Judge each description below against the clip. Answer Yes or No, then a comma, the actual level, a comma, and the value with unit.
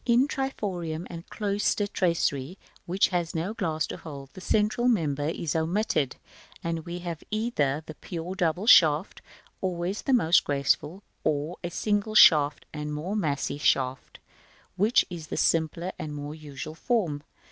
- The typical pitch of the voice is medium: Yes, medium, 170 Hz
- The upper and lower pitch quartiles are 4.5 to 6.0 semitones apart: Yes, average, 4.8 semitones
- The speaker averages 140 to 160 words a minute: Yes, average, 145 wpm